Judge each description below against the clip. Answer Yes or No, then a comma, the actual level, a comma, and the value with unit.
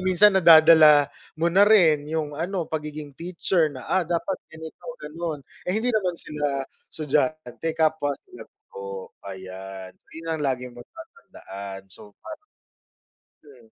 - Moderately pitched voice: Yes, medium, 155 Hz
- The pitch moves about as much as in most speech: Yes, average, 4.3 semitones